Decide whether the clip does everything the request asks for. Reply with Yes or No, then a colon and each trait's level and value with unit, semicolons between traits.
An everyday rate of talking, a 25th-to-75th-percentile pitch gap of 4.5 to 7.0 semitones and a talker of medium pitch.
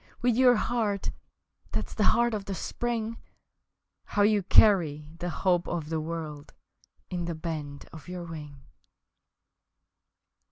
No: slow, 130 wpm; average, 5.3 semitones; medium, 175 Hz